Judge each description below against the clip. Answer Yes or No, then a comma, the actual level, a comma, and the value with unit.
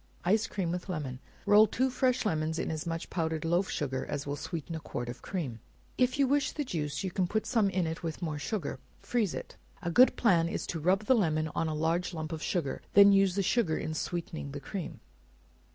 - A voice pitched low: No, medium, 170 Hz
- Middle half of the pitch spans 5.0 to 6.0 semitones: No, average, 4.5 semitones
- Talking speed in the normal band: No, fast, 225 wpm